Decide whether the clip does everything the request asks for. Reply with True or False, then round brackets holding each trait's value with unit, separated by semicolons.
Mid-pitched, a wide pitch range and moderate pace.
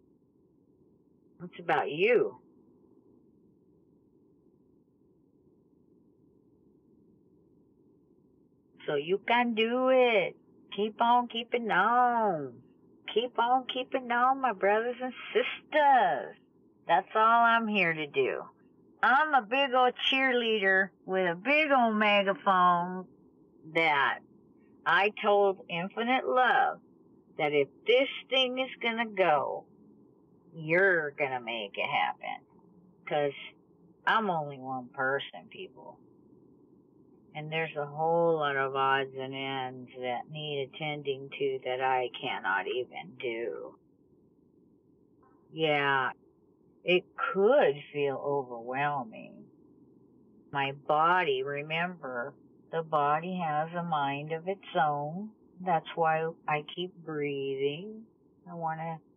False (180 Hz; 8.4 semitones; 100 wpm)